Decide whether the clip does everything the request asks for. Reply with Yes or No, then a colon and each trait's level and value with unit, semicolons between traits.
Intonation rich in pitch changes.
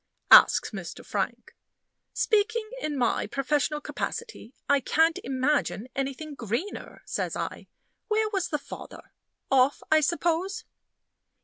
Yes: wide, 5.8 semitones